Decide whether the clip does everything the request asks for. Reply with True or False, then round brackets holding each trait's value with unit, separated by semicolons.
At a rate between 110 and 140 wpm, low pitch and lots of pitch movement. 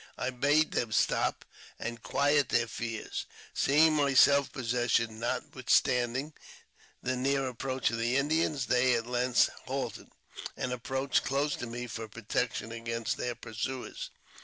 False (135 wpm; 125 Hz; 2.8 semitones)